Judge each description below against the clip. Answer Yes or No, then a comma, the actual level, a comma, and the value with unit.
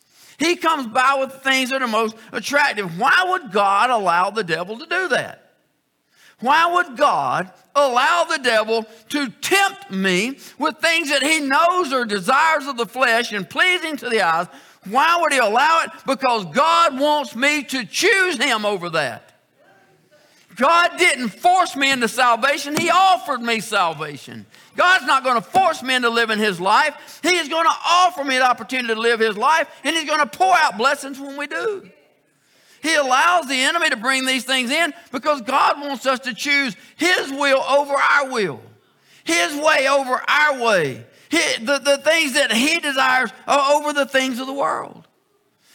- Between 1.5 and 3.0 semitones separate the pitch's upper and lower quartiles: No, average, 4.7 semitones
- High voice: Yes, very high, 280 Hz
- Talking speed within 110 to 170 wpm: No, average, 180 wpm